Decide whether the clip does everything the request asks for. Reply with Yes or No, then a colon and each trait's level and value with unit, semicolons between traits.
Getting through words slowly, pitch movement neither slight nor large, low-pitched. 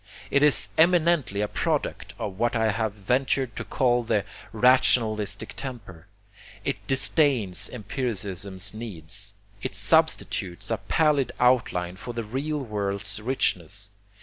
Yes: slow, 120 wpm; average, 4.7 semitones; low, 110 Hz